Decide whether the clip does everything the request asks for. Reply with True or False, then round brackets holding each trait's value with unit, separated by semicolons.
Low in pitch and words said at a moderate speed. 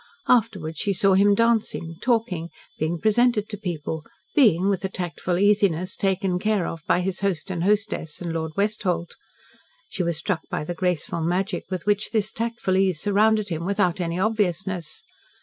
False (190 Hz; 165 wpm)